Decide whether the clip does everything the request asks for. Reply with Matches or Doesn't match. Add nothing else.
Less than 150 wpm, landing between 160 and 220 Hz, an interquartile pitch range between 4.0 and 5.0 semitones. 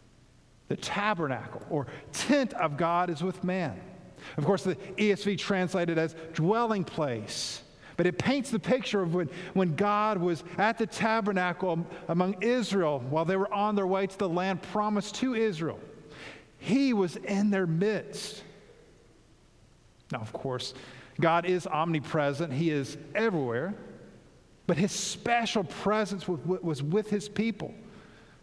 Matches